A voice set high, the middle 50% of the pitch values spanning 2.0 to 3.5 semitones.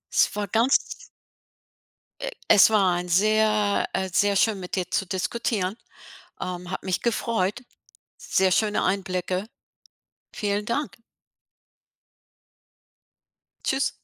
Yes: high, 200 Hz; average, 2.8 semitones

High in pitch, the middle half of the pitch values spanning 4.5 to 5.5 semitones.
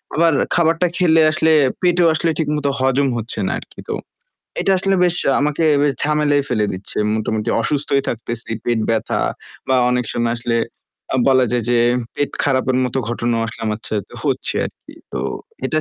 No: low, 135 Hz; average, 4.8 semitones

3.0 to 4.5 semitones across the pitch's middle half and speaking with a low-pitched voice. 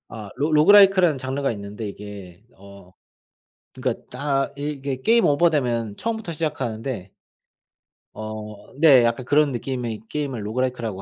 No: wide, 5.5 semitones; low, 130 Hz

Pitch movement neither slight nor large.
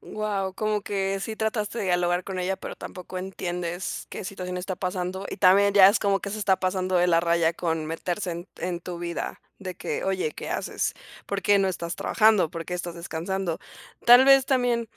No: narrow, 2.3 semitones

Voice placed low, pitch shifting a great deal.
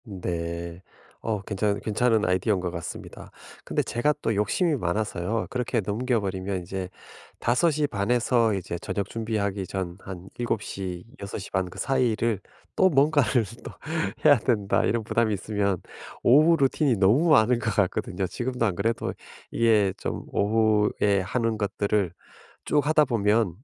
No: low, 105 Hz; average, 3.9 semitones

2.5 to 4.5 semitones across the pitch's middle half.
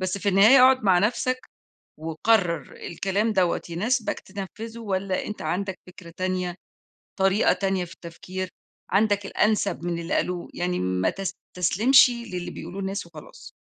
Yes: average, 3.0 semitones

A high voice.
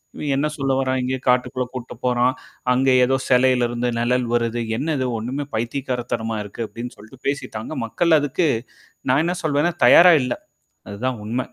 No: low, 125 Hz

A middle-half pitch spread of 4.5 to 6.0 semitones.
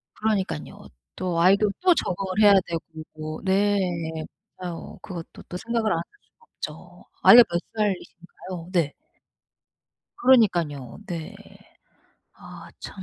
No: average, 3.9 semitones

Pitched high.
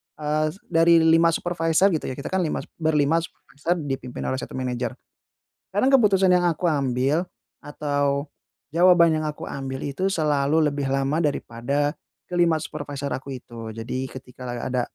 No: medium, 150 Hz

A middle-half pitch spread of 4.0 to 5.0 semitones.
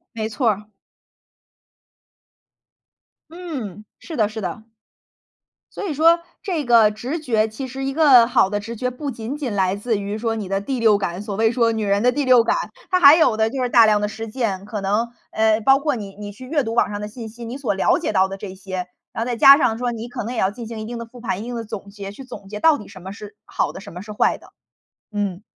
No: average, 3.5 semitones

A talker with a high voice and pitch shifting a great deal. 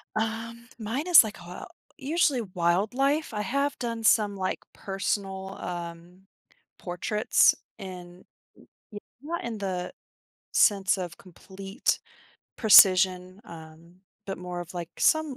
No: high, 195 Hz; average, 4.2 semitones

